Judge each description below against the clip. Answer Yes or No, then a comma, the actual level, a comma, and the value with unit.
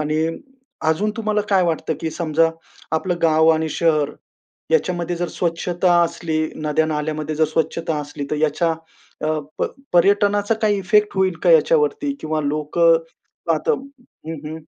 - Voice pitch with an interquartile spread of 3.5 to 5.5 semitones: Yes, average, 3.9 semitones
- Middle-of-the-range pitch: Yes, medium, 165 Hz